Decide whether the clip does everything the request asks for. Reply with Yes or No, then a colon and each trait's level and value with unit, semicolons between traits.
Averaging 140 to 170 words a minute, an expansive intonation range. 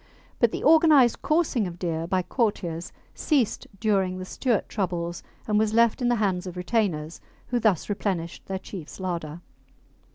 No: average, 160 wpm; average, 4.9 semitones